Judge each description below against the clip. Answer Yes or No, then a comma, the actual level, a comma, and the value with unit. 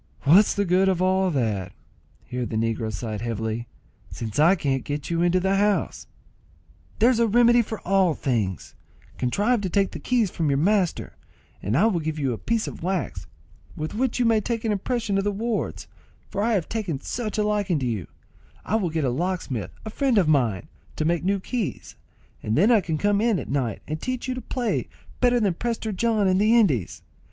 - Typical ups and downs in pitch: No, wide, 7.6 semitones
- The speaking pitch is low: No, high, 190 Hz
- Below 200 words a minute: No, fast, 205 wpm